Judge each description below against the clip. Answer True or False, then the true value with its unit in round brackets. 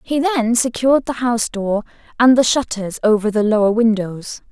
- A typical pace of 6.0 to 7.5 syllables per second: False (5.1 syllables/s)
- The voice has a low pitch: False (230 Hz)